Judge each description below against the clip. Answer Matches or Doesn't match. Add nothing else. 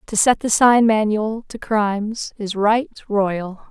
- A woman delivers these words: Matches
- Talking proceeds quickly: Doesn't match